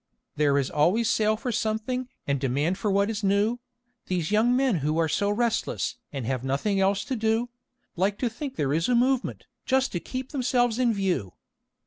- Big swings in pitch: Yes, wide, 6.6 semitones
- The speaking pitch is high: Yes, high, 210 Hz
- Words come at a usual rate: Yes, average, 190 wpm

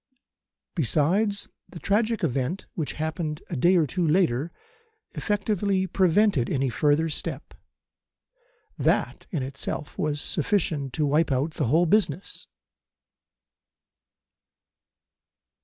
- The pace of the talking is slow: Yes, slow, 105 wpm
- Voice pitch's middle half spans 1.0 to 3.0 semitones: No, average, 4.6 semitones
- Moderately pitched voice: Yes, medium, 160 Hz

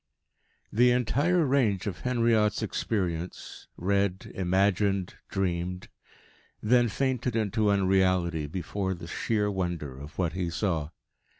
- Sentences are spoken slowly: Yes, slow, 115 wpm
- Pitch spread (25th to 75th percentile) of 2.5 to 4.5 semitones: Yes, average, 3.9 semitones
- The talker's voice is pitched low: Yes, very low, 95 Hz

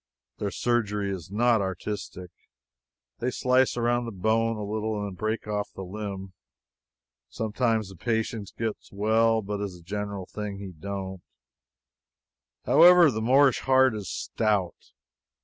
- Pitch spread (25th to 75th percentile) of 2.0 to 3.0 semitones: Yes, narrow, 2.6 semitones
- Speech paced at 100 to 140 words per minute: Yes, slow, 135 wpm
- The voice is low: Yes, low, 105 Hz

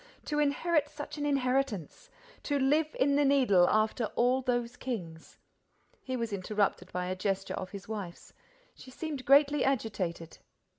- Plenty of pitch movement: Yes, wide, 6.2 semitones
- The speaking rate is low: No, average, 150 wpm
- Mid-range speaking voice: No, very high, 250 Hz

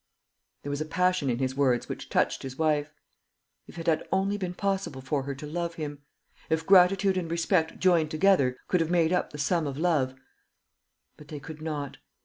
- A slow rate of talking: No, average, 195 wpm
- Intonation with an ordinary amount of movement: Yes, average, 3.8 semitones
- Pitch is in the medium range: Yes, medium, 160 Hz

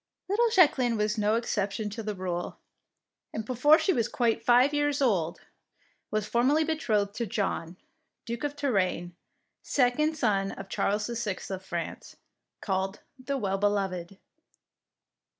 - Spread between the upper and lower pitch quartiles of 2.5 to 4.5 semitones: No, average, 4.9 semitones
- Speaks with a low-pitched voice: No, high, 215 Hz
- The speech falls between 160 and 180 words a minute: No, average, 140 wpm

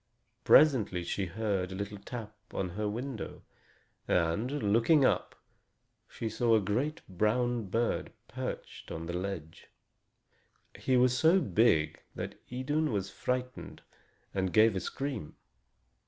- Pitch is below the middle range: Yes, low, 110 Hz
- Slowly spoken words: Yes, slow, 125 wpm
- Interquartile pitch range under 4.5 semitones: No, average, 4.9 semitones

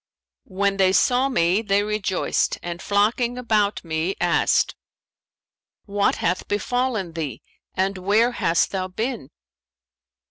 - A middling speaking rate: No, slow, 115 wpm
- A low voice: No, high, 200 Hz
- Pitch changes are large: No, average, 3.2 semitones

